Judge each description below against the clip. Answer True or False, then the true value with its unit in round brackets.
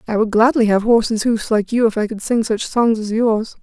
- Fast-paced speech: True (265 wpm)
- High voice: True (220 Hz)